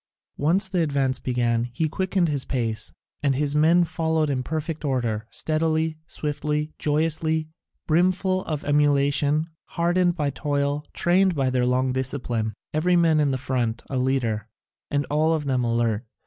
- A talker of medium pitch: Yes, medium, 145 Hz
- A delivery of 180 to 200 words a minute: No, average, 150 wpm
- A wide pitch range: No, average, 3.6 semitones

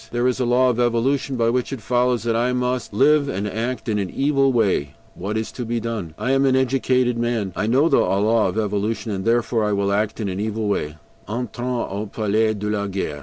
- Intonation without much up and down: No, average, 3.2 semitones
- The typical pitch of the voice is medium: No, low, 115 Hz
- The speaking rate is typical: No, fast, 230 wpm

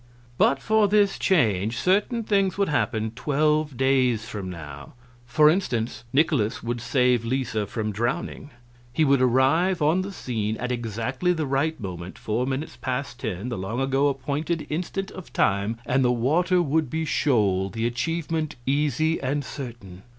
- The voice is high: No, low, 130 Hz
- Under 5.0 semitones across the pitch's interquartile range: No, wide, 5.6 semitones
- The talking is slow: No, average, 160 wpm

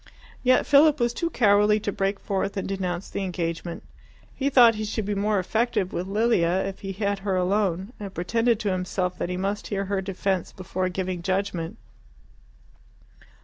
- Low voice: No, high, 195 Hz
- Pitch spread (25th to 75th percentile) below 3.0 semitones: Yes, narrow, 2.5 semitones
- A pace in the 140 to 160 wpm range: No, average, 175 wpm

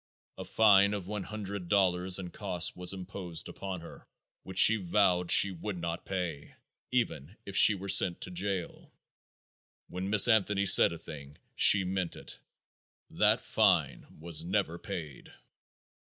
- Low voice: Yes, very low, 95 Hz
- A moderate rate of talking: Yes, average, 150 wpm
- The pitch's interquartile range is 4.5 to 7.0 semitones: No, narrow, 2.4 semitones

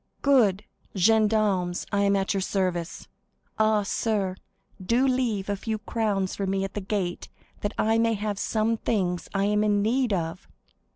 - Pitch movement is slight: Yes, narrow, 2.3 semitones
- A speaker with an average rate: Yes, average, 165 wpm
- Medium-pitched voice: No, high, 205 Hz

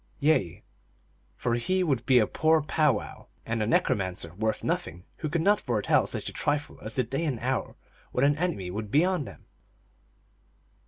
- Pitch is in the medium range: No, low, 130 Hz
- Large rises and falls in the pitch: Yes, wide, 6.2 semitones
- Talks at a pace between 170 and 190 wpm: Yes, average, 175 wpm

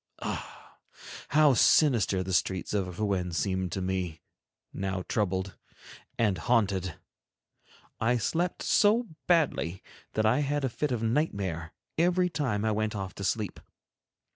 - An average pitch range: No, wide, 6.4 semitones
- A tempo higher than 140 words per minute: No, slow, 135 wpm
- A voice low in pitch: Yes, low, 105 Hz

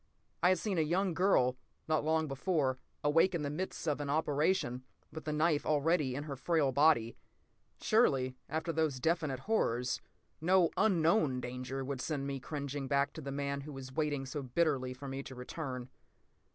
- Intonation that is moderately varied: Yes, average, 3.3 semitones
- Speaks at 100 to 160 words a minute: No, average, 180 wpm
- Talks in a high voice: No, medium, 145 Hz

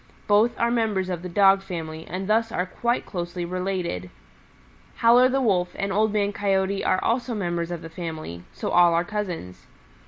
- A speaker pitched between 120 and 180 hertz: No, high, 190 Hz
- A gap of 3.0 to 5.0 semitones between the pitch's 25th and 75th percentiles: Yes, average, 3.5 semitones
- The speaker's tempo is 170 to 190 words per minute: Yes, average, 180 wpm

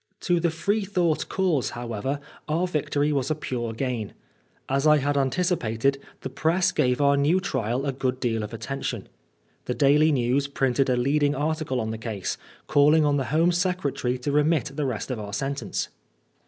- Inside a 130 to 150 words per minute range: No, average, 175 wpm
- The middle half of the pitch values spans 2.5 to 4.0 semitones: Yes, average, 3.7 semitones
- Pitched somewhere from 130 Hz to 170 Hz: Yes, medium, 140 Hz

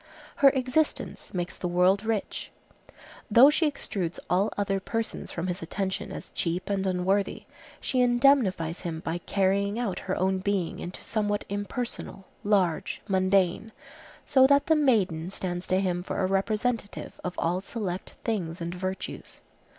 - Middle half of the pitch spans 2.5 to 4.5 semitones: Yes, average, 3.7 semitones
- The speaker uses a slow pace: No, average, 150 wpm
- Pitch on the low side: No, high, 195 Hz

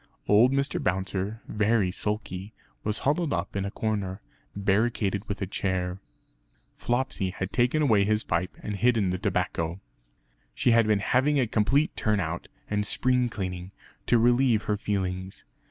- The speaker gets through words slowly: No, average, 155 wpm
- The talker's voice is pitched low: Yes, low, 105 Hz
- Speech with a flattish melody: No, average, 4.0 semitones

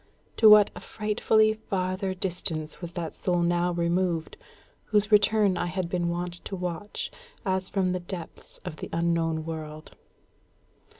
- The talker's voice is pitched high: No, medium, 180 Hz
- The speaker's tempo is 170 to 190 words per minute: No, average, 145 wpm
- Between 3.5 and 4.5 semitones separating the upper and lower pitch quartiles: No, narrow, 2.4 semitones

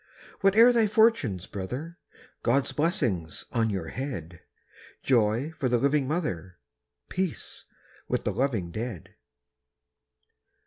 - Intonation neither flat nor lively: No, wide, 8.7 semitones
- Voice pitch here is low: Yes, low, 130 Hz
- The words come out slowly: Yes, slow, 105 wpm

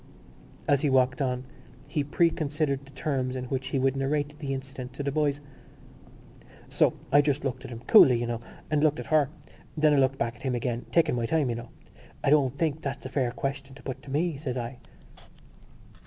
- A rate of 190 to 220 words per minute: Yes, fast, 205 wpm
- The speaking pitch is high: No, low, 135 Hz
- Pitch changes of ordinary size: No, narrow, 2.3 semitones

